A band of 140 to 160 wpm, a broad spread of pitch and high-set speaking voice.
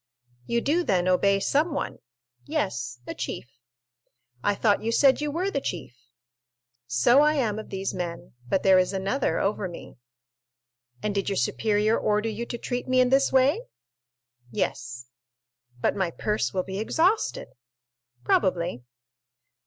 Yes: average, 145 wpm; wide, 5.9 semitones; high, 205 Hz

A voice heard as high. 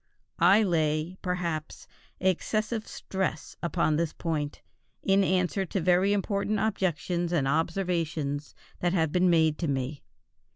No: medium, 175 Hz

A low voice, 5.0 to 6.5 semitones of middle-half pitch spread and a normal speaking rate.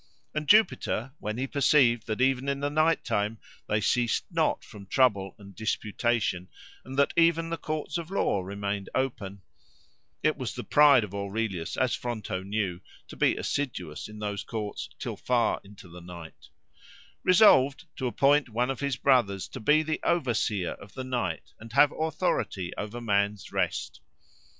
Yes: low, 120 Hz; wide, 5.6 semitones; average, 165 wpm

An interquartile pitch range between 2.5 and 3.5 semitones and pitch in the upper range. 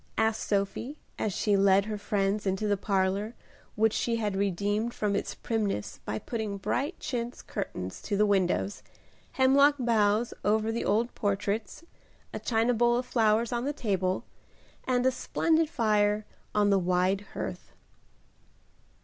Yes: average, 3.0 semitones; high, 210 Hz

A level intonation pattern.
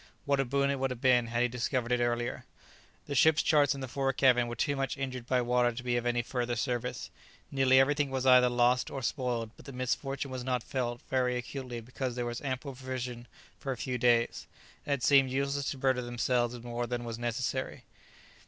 Yes: narrow, 1.8 semitones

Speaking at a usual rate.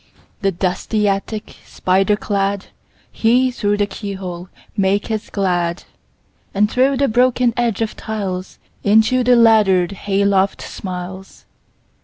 No: slow, 105 wpm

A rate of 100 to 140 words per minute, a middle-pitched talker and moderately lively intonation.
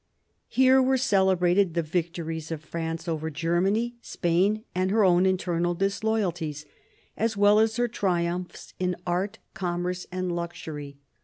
Yes: slow, 135 wpm; medium, 180 Hz; average, 3.1 semitones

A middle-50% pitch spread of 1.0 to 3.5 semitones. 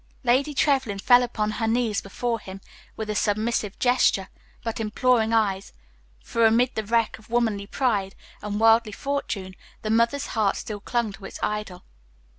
Yes: narrow, 2.5 semitones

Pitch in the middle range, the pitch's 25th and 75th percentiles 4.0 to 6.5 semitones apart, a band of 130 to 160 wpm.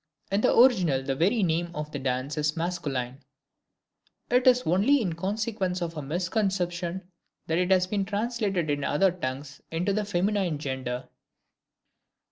Yes: medium, 175 Hz; average, 5.0 semitones; average, 150 wpm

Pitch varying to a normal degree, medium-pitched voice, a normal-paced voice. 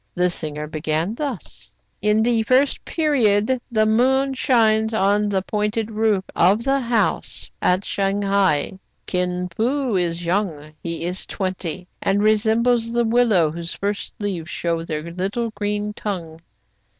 No: average, 4.2 semitones; high, 205 Hz; average, 150 wpm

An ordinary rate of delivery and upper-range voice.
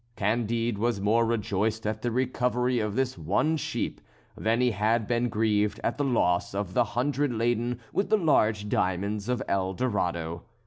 No: average, 170 wpm; low, 115 Hz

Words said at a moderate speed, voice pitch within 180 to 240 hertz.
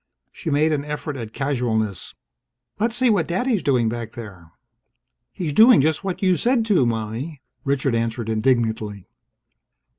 No: average, 145 wpm; low, 135 Hz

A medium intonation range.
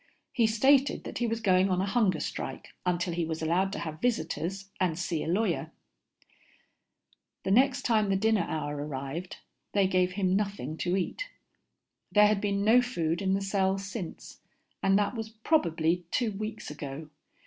Yes: average, 4.1 semitones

